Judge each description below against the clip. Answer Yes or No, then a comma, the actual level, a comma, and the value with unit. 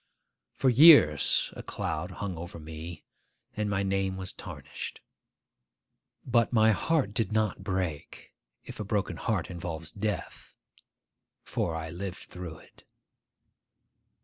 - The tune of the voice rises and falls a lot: No, average, 4.3 semitones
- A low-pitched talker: Yes, very low, 95 Hz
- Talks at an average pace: No, slow, 120 wpm